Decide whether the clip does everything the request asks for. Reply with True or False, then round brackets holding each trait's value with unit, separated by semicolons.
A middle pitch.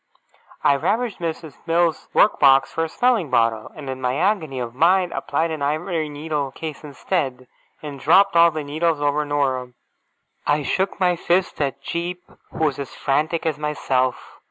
True (155 Hz)